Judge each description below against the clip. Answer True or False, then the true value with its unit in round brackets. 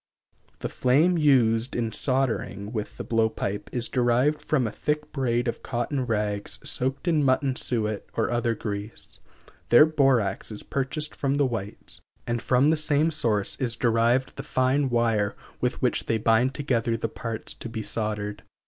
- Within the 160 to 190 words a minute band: True (165 wpm)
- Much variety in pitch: False (3.3 semitones)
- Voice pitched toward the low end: True (120 Hz)